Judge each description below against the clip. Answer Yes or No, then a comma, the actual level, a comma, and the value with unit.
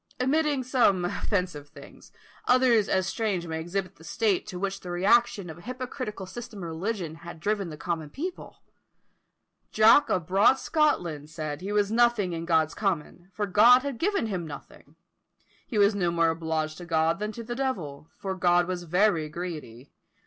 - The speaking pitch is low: No, high, 190 Hz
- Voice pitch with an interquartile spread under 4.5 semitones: No, average, 5.2 semitones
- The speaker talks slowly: No, average, 175 wpm